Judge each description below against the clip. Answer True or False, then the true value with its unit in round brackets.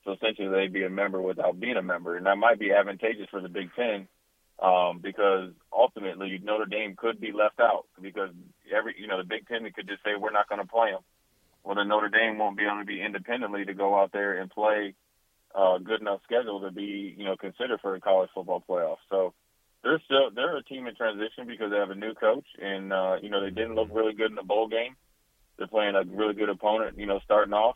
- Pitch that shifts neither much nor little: False (1.9 semitones)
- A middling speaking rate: False (240 wpm)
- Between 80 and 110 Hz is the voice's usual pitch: True (100 Hz)